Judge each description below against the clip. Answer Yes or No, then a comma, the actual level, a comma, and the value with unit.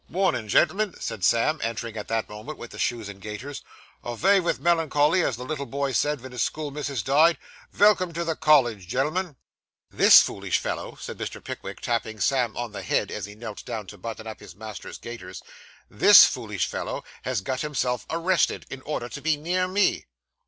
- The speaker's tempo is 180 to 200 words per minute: Yes, average, 190 wpm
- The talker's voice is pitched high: No, low, 130 Hz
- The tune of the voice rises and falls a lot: Yes, wide, 5.9 semitones